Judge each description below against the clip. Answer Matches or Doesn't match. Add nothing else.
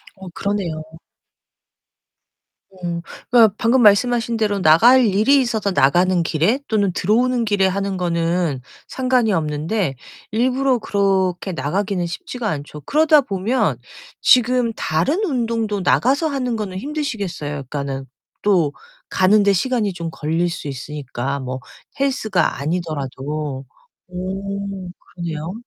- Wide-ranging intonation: Matches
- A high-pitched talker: Matches